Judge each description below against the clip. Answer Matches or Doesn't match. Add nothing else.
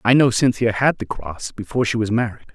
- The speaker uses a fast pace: Matches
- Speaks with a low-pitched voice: Matches